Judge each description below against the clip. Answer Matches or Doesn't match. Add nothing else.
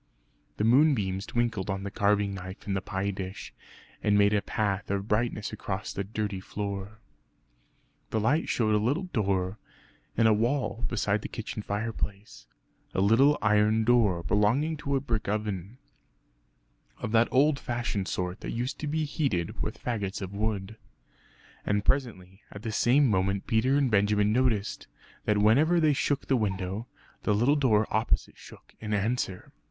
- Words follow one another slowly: Doesn't match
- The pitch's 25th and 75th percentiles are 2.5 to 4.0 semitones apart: Matches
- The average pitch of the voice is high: Doesn't match